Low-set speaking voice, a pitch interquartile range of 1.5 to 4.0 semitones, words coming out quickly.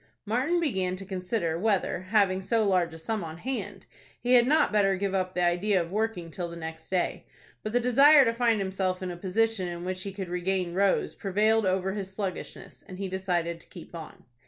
No: high, 190 Hz; average, 3.3 semitones; fast, 210 wpm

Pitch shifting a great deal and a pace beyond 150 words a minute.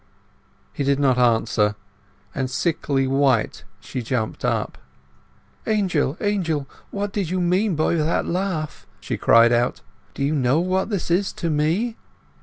No: wide, 5.9 semitones; average, 145 wpm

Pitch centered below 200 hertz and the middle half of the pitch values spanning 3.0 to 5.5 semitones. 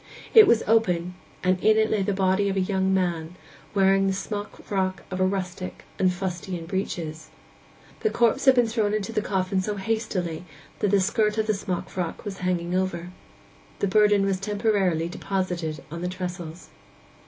No: high, 190 Hz; narrow, 2.5 semitones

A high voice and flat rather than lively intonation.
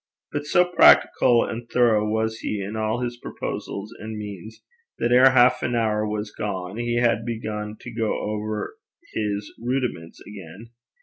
No: low, 110 Hz; narrow, 2.3 semitones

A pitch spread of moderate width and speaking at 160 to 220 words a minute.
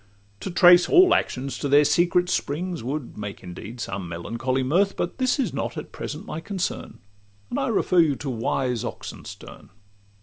No: wide, 6.3 semitones; average, 170 wpm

